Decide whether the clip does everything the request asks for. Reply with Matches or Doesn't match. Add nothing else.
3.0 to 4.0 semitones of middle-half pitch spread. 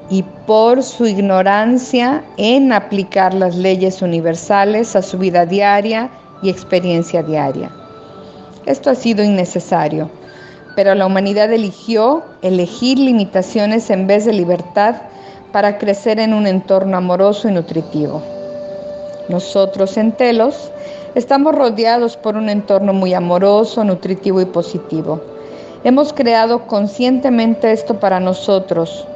Matches